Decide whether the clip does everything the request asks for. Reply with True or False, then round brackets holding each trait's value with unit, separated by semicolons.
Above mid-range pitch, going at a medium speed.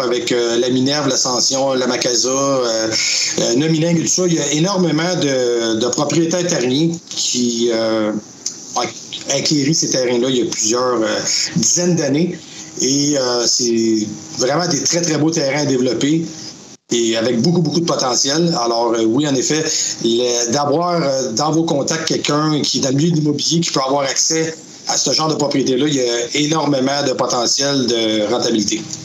False (140 Hz; 180 wpm)